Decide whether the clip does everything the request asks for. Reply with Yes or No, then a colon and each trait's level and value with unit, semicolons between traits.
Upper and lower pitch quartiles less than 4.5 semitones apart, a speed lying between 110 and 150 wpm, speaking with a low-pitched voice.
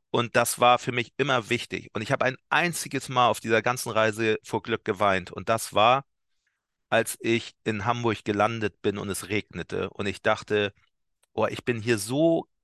No: average, 2.8 semitones; fast, 190 wpm; low, 115 Hz